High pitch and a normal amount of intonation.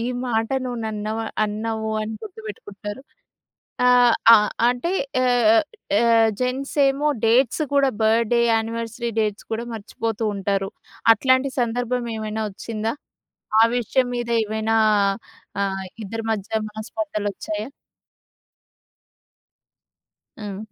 No: high, 225 Hz; narrow, 2.3 semitones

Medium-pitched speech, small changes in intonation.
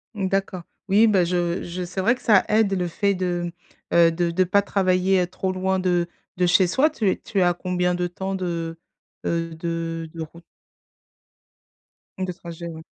Yes: medium, 180 Hz; narrow, 1.9 semitones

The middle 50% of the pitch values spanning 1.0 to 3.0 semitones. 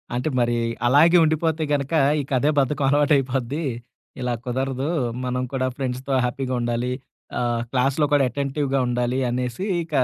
Yes: narrow, 2.6 semitones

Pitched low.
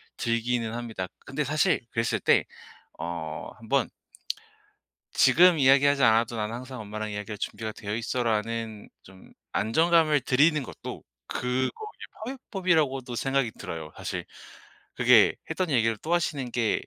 Yes: low, 120 Hz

